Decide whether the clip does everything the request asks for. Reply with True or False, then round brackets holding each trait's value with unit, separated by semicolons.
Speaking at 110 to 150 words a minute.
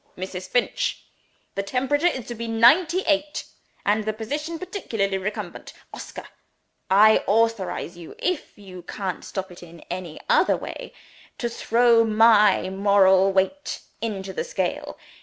True (140 wpm)